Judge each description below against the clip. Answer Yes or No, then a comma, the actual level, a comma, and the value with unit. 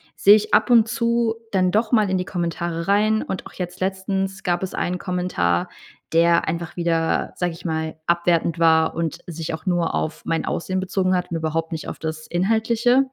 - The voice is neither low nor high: Yes, medium, 180 Hz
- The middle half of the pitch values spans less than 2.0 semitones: No, average, 2.8 semitones